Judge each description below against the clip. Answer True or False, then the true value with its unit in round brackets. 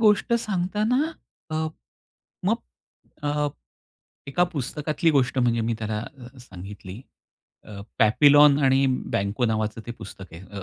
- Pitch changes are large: True (5.8 semitones)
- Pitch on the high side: False (130 Hz)